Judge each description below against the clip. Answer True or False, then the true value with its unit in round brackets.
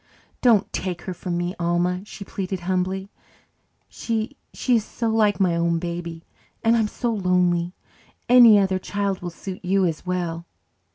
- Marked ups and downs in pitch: False (2.9 semitones)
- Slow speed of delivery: False (160 wpm)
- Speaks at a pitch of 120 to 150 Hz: False (185 Hz)